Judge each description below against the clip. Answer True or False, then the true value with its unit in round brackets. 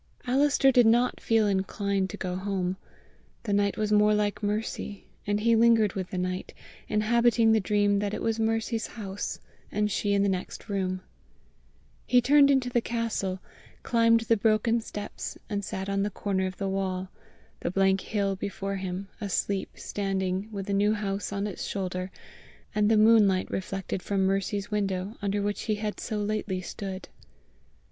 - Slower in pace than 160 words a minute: False (170 wpm)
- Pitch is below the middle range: False (205 Hz)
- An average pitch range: False (2.3 semitones)